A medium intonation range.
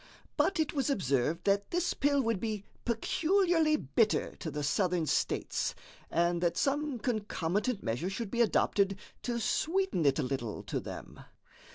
No: wide, 8.6 semitones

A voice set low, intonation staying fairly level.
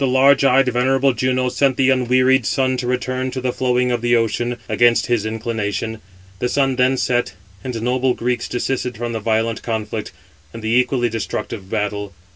Yes: low, 125 Hz; narrow, 2.1 semitones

